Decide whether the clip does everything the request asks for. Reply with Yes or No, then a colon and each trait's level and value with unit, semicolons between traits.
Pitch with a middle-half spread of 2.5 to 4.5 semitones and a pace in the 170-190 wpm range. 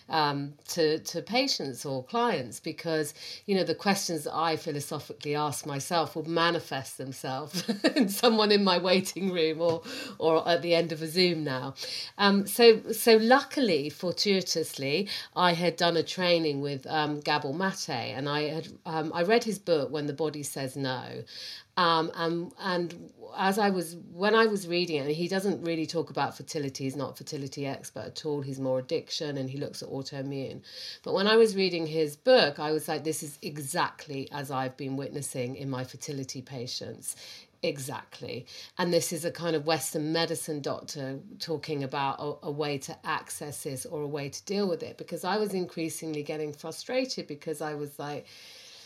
Yes: average, 3.5 semitones; average, 185 wpm